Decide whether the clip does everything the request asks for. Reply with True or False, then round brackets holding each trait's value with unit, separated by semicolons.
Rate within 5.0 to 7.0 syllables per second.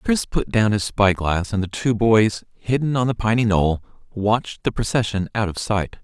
False (4.8 syllables/s)